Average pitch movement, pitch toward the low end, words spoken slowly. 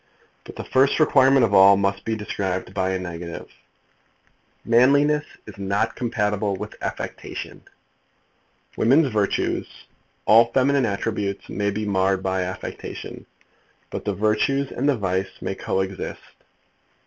Yes: average, 4.7 semitones; low, 105 Hz; slow, 130 wpm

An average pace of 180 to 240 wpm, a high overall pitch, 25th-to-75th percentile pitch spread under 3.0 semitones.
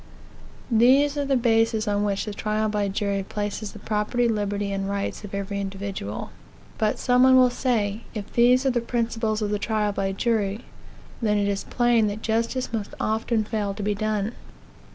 Yes: average, 185 wpm; high, 215 Hz; narrow, 2.5 semitones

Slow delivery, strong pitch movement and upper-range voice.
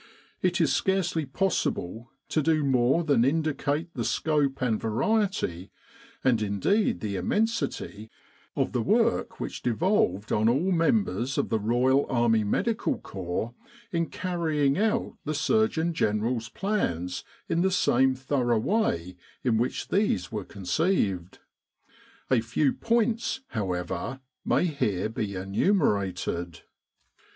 No: slow, 125 wpm; wide, 8.3 semitones; low, 130 Hz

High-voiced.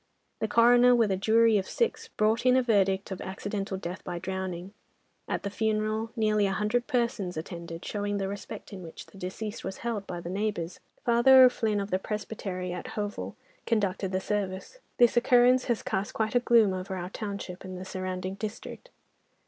Yes: high, 205 Hz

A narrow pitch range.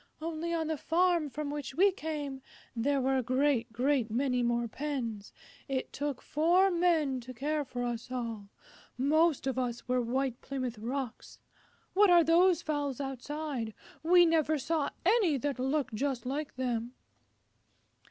No: average, 3.9 semitones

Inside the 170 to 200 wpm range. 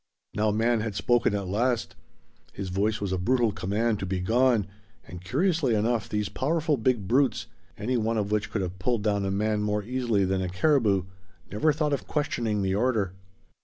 Yes: average, 190 wpm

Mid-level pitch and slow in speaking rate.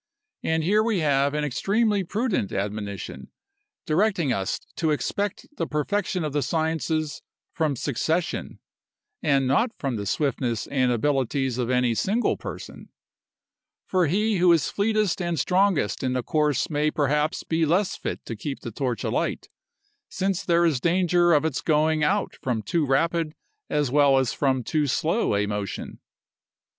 No: medium, 155 Hz; average, 155 wpm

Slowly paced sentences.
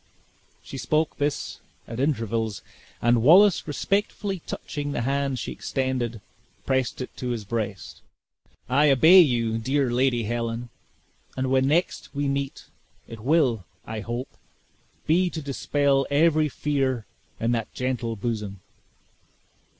Yes: slow, 125 wpm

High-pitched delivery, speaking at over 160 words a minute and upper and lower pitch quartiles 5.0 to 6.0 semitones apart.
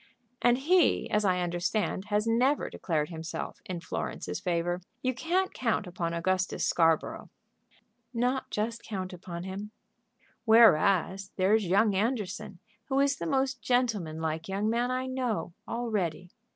No: high, 205 Hz; average, 140 wpm; wide, 5.4 semitones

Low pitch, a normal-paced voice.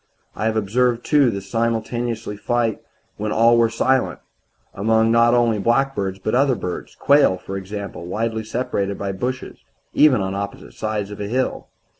Yes: low, 110 Hz; average, 165 wpm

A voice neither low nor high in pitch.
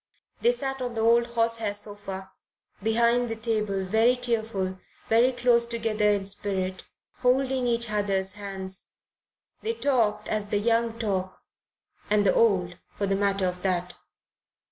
No: high, 215 Hz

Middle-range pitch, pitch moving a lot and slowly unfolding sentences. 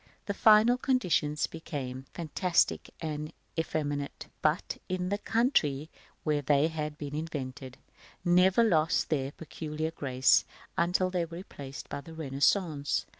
No: medium, 155 Hz; average, 3.8 semitones; slow, 125 wpm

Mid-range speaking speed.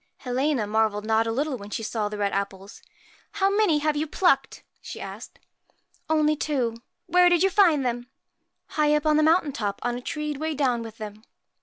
No: fast, 215 wpm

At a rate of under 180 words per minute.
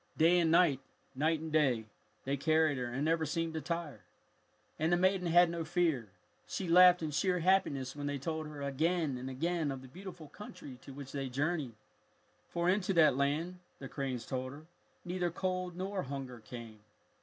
No: average, 185 wpm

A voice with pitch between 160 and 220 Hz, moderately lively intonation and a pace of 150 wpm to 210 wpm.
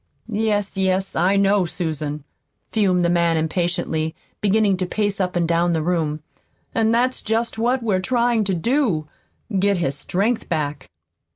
Yes: medium, 185 Hz; average, 4.4 semitones; average, 155 wpm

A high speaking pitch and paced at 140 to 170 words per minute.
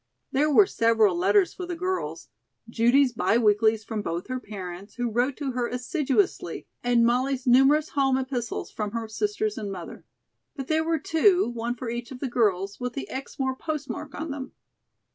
No: very high, 250 Hz; average, 180 wpm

